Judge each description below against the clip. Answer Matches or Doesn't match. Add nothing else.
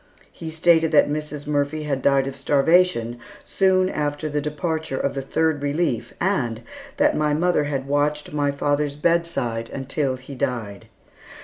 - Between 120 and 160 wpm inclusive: Matches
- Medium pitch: Matches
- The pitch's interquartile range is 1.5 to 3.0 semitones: Matches